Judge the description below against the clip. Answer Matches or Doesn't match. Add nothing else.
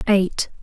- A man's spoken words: Doesn't match